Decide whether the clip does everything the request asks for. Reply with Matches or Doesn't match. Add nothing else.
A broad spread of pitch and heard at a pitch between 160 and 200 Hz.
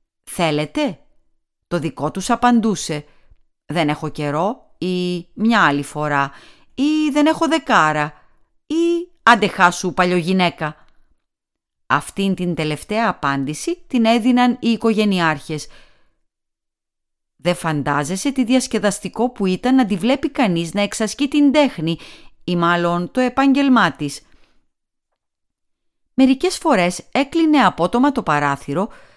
Matches